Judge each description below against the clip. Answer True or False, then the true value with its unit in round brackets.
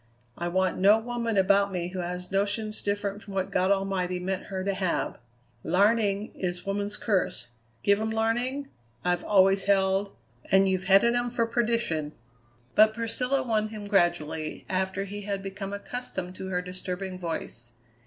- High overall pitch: True (195 Hz)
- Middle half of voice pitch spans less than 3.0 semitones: True (2.6 semitones)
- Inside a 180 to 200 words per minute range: False (160 wpm)